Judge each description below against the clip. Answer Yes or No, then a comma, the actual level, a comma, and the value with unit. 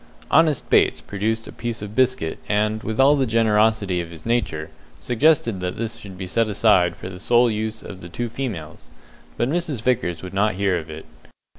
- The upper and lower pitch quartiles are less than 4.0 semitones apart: No, average, 4.4 semitones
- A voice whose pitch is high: No, low, 110 Hz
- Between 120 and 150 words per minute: No, average, 195 wpm